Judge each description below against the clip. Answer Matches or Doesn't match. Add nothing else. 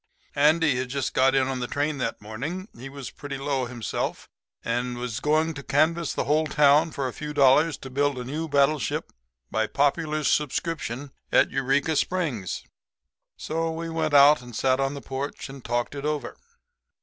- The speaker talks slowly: Doesn't match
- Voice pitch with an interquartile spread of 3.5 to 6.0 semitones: Doesn't match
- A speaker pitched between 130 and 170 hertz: Matches